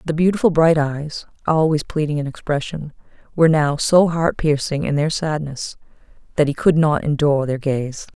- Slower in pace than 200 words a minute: Yes, average, 170 wpm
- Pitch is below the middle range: No, medium, 150 Hz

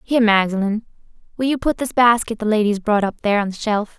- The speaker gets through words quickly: Yes, fast, 225 wpm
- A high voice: Yes, high, 220 Hz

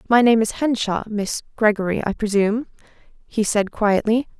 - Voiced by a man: No, female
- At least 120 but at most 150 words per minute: Yes, slow, 135 wpm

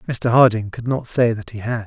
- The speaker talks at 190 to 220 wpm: No, fast, 260 wpm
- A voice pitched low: Yes, low, 115 Hz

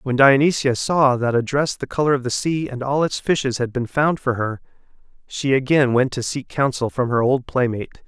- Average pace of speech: No, fast, 225 wpm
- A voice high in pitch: No, low, 130 Hz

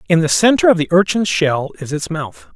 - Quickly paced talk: Yes, fast, 235 wpm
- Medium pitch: Yes, medium, 165 Hz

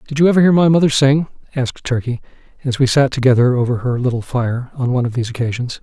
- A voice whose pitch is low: Yes, low, 130 Hz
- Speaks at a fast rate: Yes, fast, 225 wpm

